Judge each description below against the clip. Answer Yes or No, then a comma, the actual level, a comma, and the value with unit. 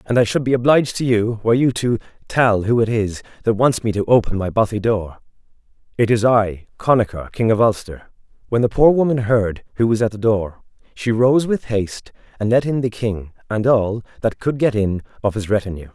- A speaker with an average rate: No, fast, 215 wpm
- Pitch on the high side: No, low, 110 Hz